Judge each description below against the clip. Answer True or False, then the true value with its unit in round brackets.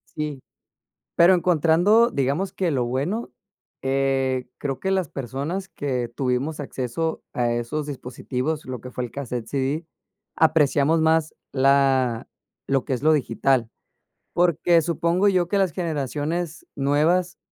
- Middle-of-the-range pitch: True (145 Hz)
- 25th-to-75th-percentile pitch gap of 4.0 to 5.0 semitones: True (4.3 semitones)